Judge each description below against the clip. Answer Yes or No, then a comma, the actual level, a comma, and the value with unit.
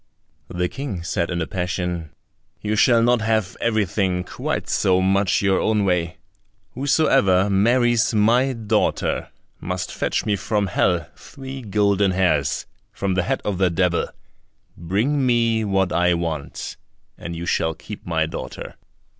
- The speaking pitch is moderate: No, very low, 95 Hz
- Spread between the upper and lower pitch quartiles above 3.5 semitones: Yes, average, 3.9 semitones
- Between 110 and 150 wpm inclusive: Yes, average, 145 wpm